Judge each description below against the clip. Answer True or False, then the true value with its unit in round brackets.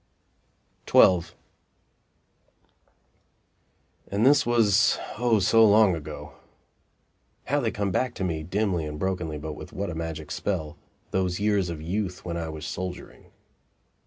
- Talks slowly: True (130 wpm)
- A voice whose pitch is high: False (90 Hz)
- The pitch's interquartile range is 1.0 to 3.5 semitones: False (4.1 semitones)